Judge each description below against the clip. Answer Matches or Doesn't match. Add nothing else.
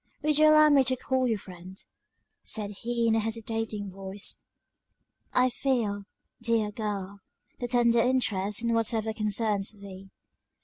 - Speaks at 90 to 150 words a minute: Matches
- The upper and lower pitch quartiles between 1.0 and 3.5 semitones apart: Matches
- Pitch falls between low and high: Doesn't match